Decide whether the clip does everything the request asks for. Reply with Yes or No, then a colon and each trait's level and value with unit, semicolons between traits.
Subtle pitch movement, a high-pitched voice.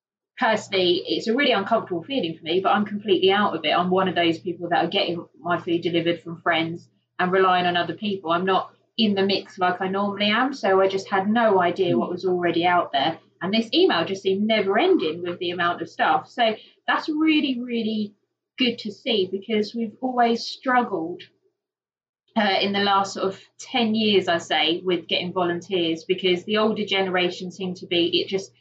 No: average, 4.3 semitones; high, 195 Hz